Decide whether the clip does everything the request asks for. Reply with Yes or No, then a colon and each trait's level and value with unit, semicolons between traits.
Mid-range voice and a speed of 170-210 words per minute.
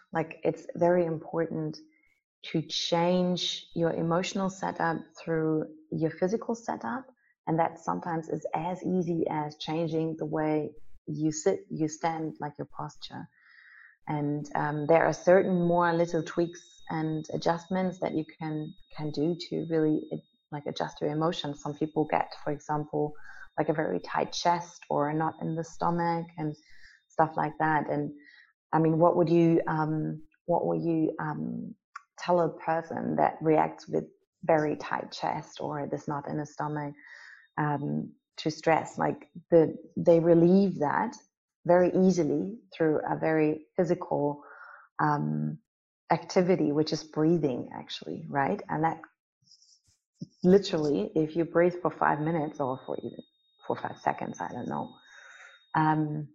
No: medium, 160 Hz; average, 145 wpm